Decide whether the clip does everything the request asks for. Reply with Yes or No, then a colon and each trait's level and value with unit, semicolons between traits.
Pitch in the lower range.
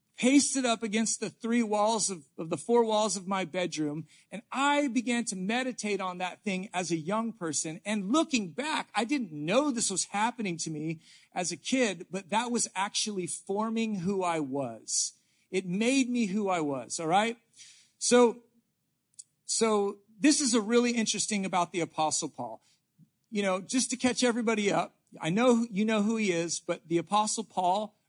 No: high, 210 Hz